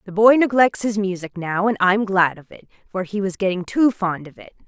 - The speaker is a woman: Yes, female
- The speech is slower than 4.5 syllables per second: No, 5.2 syllables/s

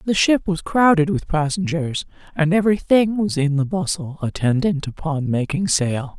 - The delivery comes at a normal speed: Yes, average, 165 wpm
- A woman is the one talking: Yes, female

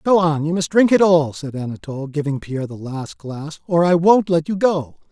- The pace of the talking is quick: Yes, fast, 235 wpm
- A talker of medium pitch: Yes, medium, 160 Hz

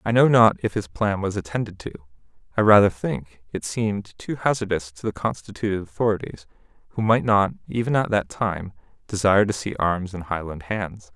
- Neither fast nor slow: Yes, average, 185 wpm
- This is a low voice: Yes, low, 100 Hz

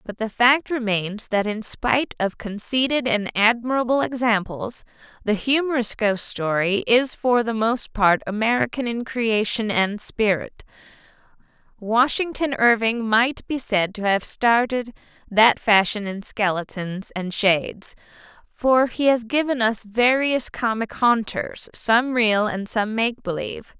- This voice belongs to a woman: Yes, female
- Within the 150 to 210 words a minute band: No, slow, 135 wpm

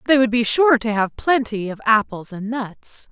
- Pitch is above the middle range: Yes, high, 230 Hz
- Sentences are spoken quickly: Yes, fast, 210 wpm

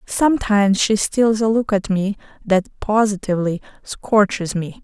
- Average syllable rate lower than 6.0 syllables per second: Yes, 4.5 syllables/s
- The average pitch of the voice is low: No, high, 205 Hz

